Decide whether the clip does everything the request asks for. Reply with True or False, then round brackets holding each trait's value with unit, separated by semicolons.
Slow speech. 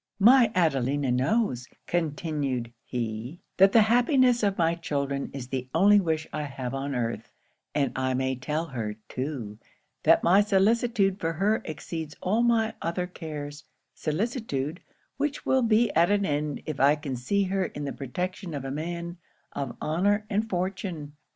False (160 wpm)